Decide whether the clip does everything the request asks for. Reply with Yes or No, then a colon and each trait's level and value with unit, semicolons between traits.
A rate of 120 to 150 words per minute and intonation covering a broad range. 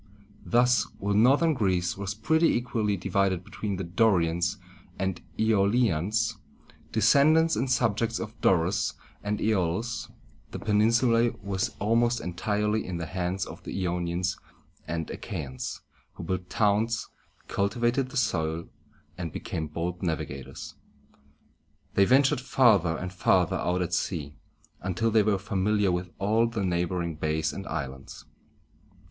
No: average, 140 wpm; average, 4.4 semitones